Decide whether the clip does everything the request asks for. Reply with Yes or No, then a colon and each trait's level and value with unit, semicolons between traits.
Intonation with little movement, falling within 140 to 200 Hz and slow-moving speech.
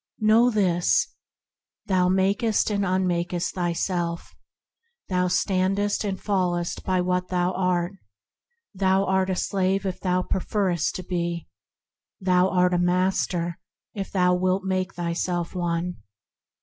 Yes: narrow, 1.4 semitones; medium, 185 Hz; slow, 125 wpm